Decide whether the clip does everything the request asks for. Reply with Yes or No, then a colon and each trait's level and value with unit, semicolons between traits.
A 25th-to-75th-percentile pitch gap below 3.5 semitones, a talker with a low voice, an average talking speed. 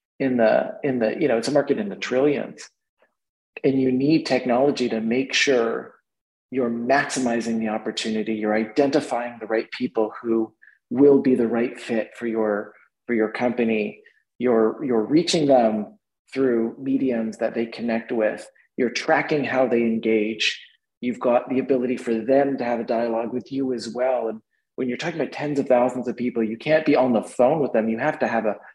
Yes: average, 2.7 semitones; low, 120 Hz; average, 190 wpm